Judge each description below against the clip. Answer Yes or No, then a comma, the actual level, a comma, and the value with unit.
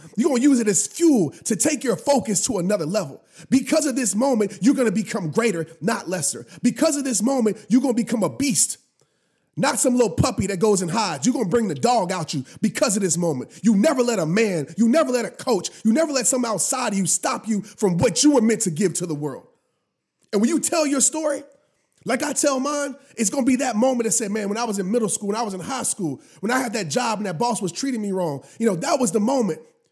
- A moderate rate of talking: No, fast, 255 wpm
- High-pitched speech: Yes, high, 225 Hz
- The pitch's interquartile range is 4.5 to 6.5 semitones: Yes, average, 5.1 semitones